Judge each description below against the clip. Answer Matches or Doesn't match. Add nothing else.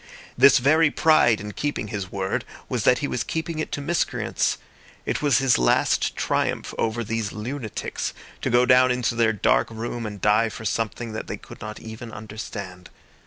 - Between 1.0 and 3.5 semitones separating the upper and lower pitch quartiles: Matches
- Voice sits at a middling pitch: Doesn't match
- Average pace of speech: Matches